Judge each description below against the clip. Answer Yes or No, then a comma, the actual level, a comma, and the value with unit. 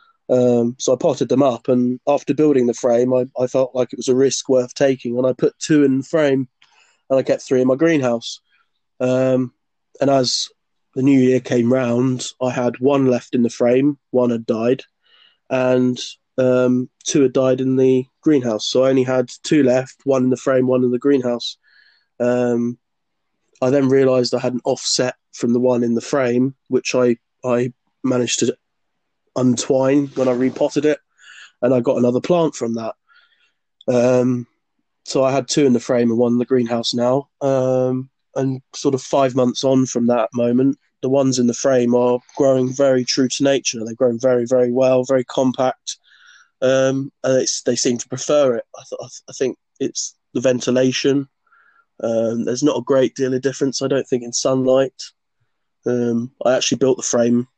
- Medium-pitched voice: No, low, 130 Hz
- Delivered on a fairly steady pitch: Yes, narrow, 1.5 semitones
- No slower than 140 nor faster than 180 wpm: No, average, 190 wpm